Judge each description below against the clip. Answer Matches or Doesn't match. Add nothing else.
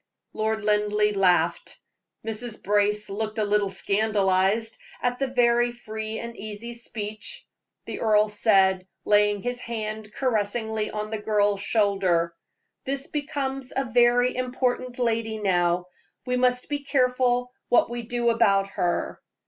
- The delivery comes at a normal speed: Doesn't match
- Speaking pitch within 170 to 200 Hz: Doesn't match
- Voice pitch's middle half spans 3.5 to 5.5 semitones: Doesn't match